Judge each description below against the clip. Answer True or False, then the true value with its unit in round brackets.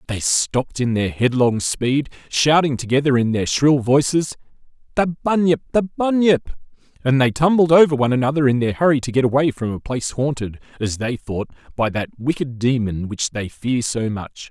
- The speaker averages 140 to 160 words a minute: False (180 wpm)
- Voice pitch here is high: False (130 Hz)